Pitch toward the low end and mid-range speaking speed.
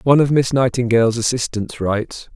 Yes: low, 120 Hz; average, 155 wpm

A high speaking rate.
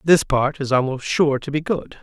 Yes: fast, 235 wpm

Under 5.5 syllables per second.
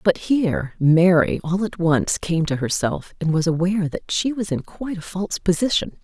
Yes: 5.1 syllables/s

